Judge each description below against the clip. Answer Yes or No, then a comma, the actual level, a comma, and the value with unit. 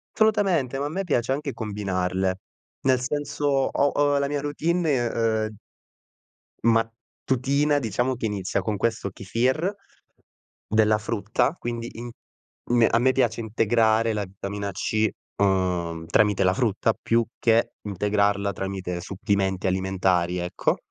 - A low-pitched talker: Yes, low, 110 Hz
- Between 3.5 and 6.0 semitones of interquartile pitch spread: Yes, average, 4.9 semitones